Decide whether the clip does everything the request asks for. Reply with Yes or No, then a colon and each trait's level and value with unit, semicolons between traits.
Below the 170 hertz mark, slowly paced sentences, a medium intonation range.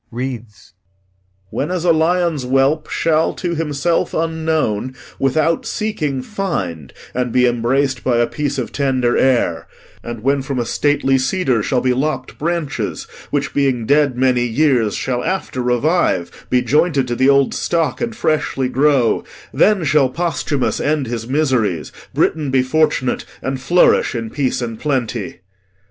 No: low, 135 Hz; average, 150 wpm; average, 3.9 semitones